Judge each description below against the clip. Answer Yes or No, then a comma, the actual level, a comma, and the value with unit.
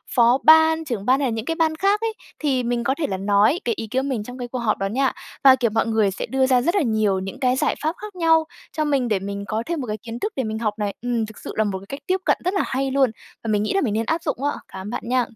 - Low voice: No, very high, 250 Hz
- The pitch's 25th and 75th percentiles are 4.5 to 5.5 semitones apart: Yes, average, 5.1 semitones